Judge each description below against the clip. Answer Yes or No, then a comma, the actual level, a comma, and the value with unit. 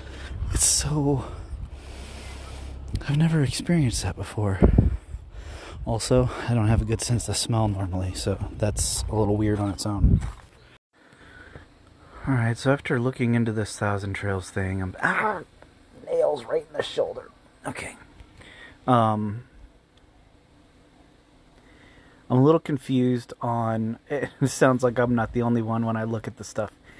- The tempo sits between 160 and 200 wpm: No, average, 140 wpm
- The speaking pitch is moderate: No, low, 110 Hz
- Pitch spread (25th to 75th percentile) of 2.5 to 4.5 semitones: No, average, 5.0 semitones